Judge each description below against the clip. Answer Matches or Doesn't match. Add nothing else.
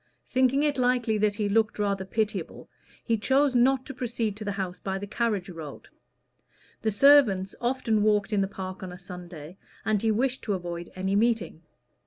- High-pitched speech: Matches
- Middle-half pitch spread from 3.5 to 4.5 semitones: Matches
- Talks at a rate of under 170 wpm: Doesn't match